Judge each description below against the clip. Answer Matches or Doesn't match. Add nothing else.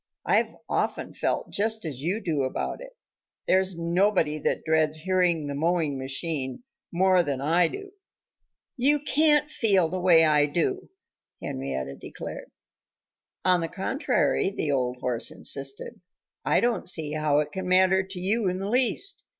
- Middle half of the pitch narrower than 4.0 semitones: Doesn't match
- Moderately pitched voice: Matches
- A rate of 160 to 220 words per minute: Doesn't match